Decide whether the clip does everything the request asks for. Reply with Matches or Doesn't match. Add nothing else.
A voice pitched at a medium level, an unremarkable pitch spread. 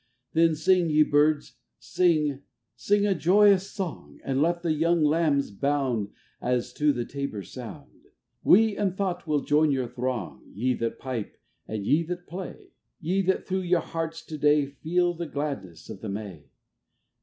Matches